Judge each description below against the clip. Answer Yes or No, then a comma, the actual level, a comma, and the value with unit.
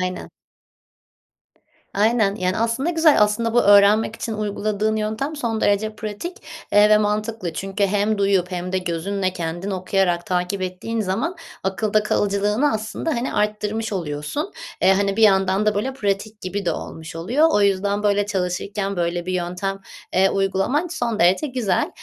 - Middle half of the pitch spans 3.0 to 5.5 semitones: No, narrow, 2.5 semitones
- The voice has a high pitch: Yes, high, 205 Hz